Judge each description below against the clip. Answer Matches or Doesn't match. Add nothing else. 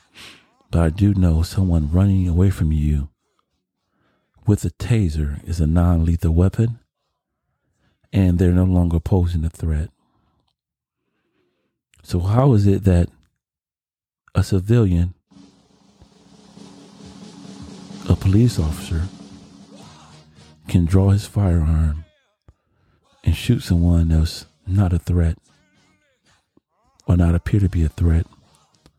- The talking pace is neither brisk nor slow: Doesn't match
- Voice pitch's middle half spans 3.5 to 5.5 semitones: Doesn't match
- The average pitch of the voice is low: Matches